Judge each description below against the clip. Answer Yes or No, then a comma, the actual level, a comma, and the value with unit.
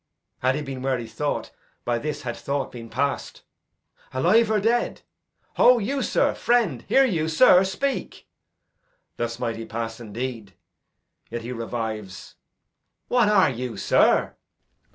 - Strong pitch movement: Yes, wide, 9.0 semitones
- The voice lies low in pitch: Yes, low, 130 Hz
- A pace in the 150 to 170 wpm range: No, average, 140 wpm